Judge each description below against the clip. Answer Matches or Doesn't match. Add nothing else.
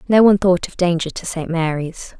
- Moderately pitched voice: Matches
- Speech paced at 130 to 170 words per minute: Doesn't match